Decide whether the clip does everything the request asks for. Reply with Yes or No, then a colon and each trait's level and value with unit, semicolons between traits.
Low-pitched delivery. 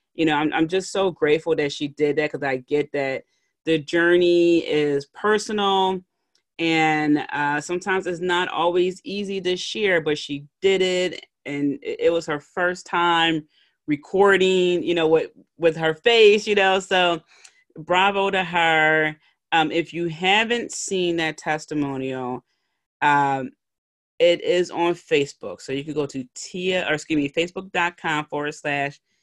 No: medium, 165 Hz